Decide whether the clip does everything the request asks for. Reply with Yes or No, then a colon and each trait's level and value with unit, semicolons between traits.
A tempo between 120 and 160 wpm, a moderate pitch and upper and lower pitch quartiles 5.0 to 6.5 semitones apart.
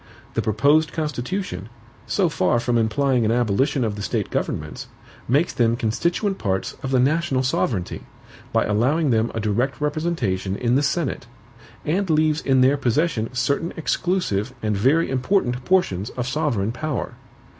No: average, 150 wpm; low, 130 Hz; wide, 5.6 semitones